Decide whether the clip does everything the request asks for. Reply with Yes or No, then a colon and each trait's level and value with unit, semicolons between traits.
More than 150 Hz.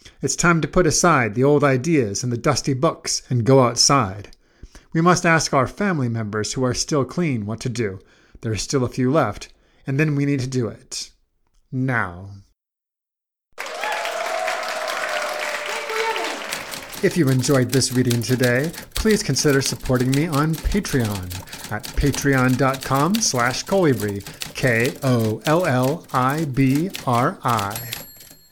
No: low, 135 Hz